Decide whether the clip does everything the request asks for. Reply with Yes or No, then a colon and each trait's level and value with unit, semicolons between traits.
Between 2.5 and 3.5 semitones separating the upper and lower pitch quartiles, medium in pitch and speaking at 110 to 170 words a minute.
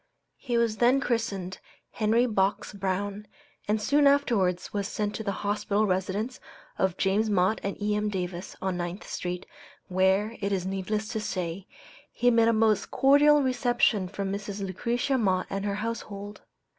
No: average, 3.1 semitones; high, 205 Hz; average, 155 wpm